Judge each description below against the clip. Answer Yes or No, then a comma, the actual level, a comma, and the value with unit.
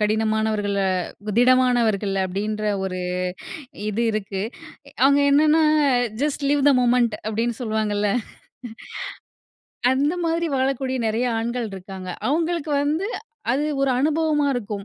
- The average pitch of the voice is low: No, high, 240 Hz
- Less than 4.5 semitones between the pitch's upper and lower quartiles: No, average, 5.1 semitones